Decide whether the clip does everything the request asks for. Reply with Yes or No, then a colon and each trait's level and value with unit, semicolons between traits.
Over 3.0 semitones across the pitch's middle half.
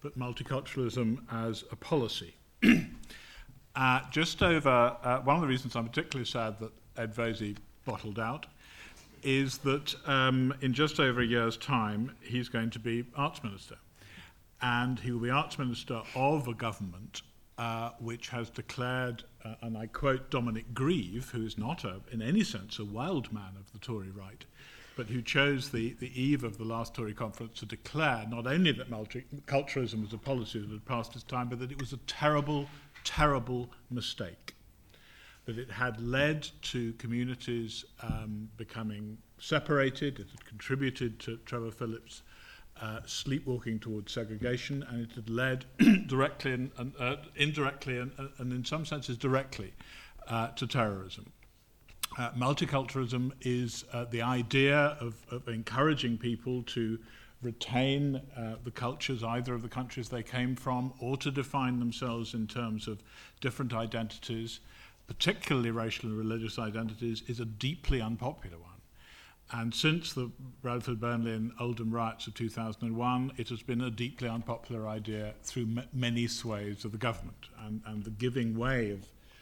No: average, 2.7 semitones